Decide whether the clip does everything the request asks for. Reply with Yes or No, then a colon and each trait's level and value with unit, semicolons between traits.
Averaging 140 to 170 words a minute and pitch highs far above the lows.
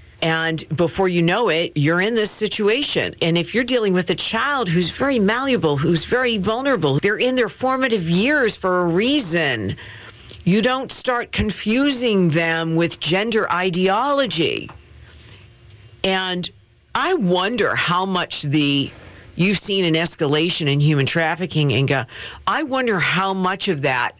Yes: average, 145 wpm; wide, 5.9 semitones